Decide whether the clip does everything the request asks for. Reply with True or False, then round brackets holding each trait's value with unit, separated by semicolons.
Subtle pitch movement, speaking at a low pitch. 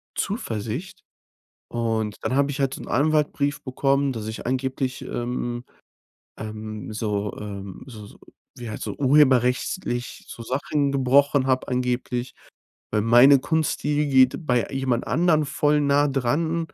False (3.4 semitones; 130 Hz)